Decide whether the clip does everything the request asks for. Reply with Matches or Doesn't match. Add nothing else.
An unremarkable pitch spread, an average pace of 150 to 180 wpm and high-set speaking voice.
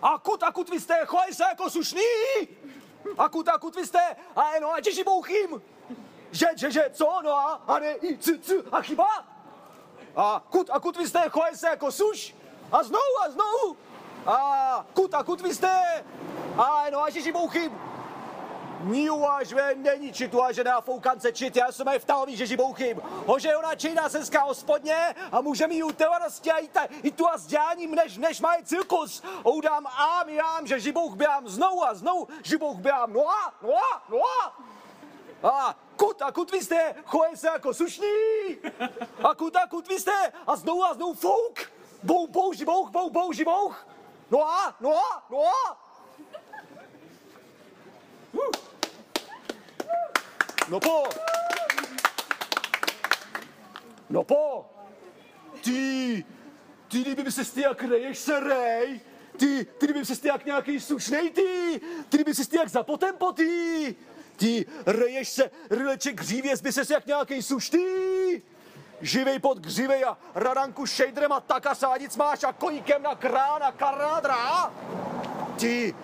Matches